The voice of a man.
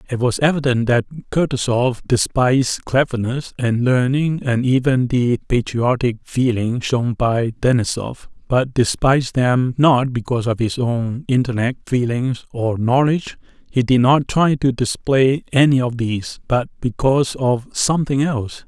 Yes: male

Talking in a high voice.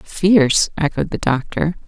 No: medium, 160 Hz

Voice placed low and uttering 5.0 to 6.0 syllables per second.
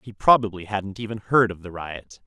Yes: low, 100 Hz; 5.1 syllables/s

